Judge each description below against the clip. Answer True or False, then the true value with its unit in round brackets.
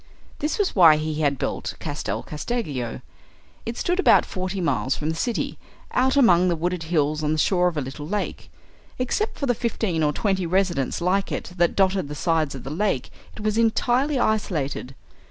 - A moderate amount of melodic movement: False (6.1 semitones)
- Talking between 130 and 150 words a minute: False (190 wpm)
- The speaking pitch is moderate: True (175 Hz)